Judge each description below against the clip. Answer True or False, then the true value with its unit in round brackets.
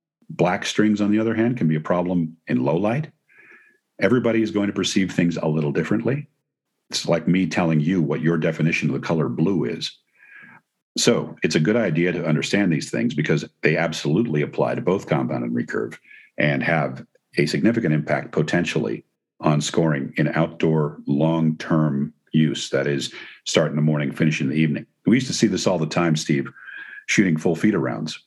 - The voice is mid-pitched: False (80 Hz)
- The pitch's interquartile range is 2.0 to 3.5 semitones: False (4.0 semitones)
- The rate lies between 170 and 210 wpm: True (190 wpm)